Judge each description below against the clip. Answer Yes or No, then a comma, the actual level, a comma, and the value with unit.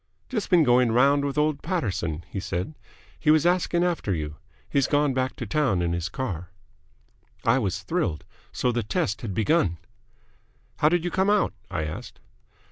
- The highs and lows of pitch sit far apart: Yes, wide, 8.8 semitones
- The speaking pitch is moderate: No, low, 125 Hz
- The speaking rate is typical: Yes, average, 175 wpm